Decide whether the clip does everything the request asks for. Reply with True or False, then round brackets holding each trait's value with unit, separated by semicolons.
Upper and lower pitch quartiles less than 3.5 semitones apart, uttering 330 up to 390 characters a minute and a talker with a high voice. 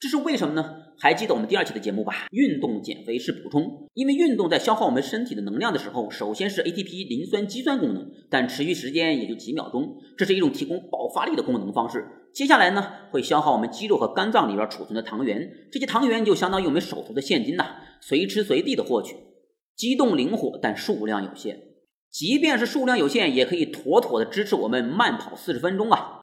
False (5.5 semitones; 355 characters per minute; 270 Hz)